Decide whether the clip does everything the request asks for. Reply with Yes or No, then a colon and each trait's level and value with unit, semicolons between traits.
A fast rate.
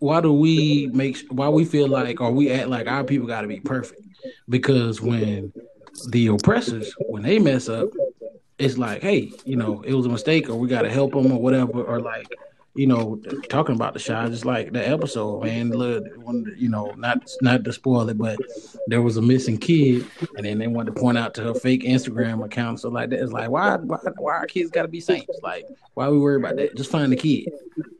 Yes: fast, 230 wpm